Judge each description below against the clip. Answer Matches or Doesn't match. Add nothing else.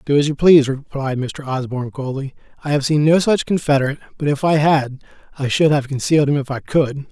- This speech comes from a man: Matches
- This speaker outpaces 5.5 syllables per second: Matches